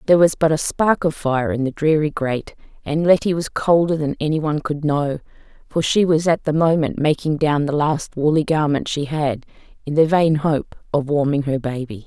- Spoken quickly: Yes, fast, 210 wpm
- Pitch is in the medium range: Yes, medium, 150 Hz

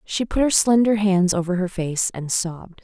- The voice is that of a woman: Yes, female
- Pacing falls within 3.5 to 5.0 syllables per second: Yes, 4.8 syllables/s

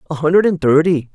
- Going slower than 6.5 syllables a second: No, 6.7 syllables/s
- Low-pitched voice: No, medium, 160 Hz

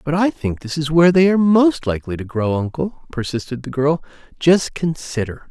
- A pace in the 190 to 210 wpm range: Yes, average, 195 wpm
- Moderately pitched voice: Yes, medium, 150 Hz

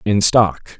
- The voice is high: No, very low, 95 Hz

